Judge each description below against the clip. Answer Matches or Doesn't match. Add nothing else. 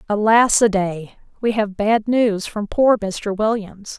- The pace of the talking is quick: Doesn't match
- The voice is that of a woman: Matches